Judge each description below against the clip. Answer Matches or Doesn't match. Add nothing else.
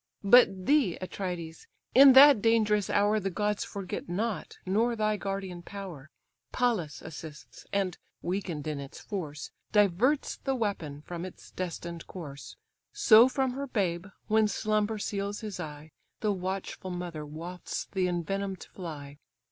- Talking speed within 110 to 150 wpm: Matches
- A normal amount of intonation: Matches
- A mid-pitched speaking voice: Doesn't match